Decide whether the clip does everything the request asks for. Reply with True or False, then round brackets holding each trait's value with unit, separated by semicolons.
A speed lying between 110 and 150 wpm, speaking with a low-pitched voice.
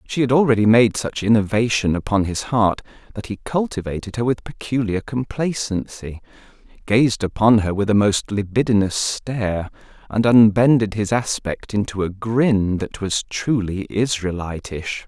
True (140 wpm; 110 Hz)